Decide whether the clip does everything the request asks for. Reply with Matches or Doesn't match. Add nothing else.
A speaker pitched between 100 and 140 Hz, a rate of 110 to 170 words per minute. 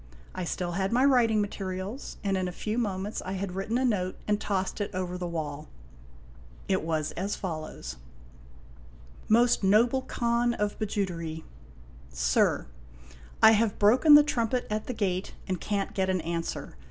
Doesn't match